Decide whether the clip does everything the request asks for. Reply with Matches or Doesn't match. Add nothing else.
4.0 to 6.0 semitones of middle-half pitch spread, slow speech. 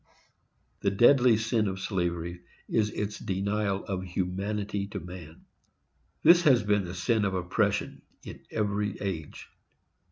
Doesn't match